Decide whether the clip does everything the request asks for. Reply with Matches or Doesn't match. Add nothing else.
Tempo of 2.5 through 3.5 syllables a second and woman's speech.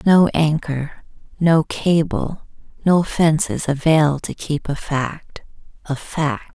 Matches